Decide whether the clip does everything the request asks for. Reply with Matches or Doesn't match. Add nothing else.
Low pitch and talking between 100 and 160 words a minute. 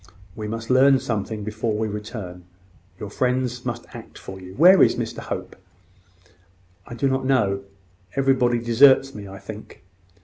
Matches